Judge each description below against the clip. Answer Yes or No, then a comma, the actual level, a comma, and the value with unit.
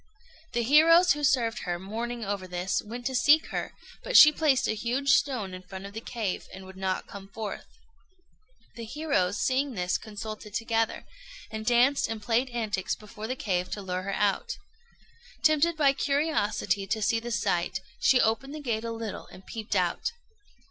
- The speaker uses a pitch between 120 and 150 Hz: No, high, 225 Hz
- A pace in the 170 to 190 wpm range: Yes, average, 180 wpm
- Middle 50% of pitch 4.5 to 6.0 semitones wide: Yes, average, 5.1 semitones